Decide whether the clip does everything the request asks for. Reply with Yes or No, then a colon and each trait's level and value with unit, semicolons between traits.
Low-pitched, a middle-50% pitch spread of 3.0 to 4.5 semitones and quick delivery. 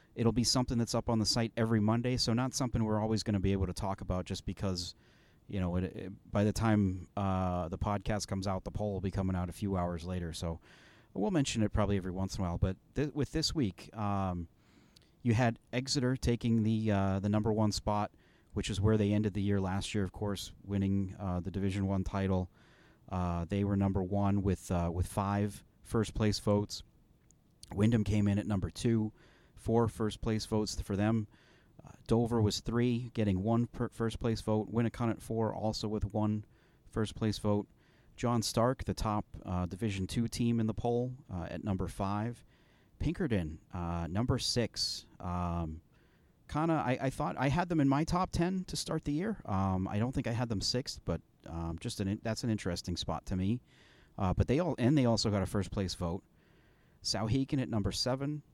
Yes: low, 105 Hz; average, 3.4 semitones; fast, 210 wpm